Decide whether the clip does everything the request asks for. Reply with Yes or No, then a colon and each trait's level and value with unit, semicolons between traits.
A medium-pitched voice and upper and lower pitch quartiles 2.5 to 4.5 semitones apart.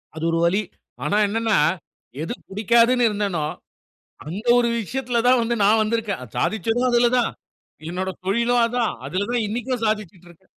No: high, 220 Hz; average, 3.3 semitones